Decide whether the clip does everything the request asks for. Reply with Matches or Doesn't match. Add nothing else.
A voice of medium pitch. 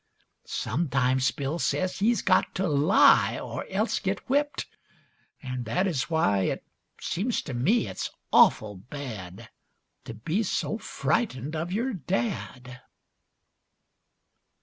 Matches